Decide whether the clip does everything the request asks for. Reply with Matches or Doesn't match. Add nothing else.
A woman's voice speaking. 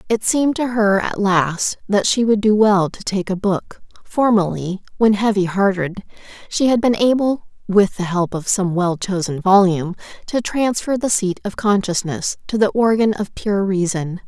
Matches